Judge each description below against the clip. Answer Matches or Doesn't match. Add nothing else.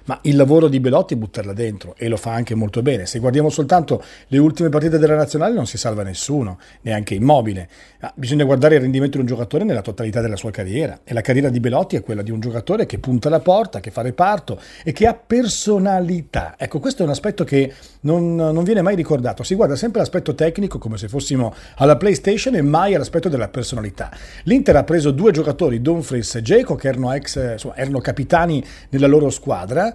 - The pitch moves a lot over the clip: Matches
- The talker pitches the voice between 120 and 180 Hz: Matches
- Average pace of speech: Doesn't match